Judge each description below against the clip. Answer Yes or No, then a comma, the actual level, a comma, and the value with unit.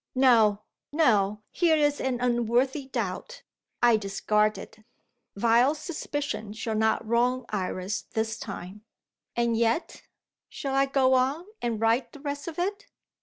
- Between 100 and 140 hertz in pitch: No, high, 240 Hz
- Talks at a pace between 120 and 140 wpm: Yes, slow, 135 wpm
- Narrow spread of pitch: No, average, 4.2 semitones